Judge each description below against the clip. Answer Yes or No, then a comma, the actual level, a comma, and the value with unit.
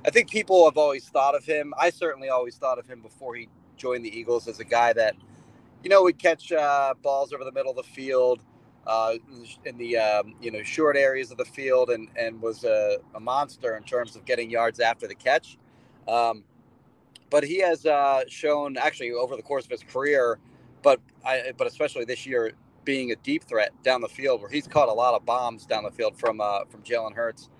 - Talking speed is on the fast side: Yes, fast, 220 wpm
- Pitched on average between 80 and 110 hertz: No, low, 135 Hz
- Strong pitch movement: Yes, wide, 6.5 semitones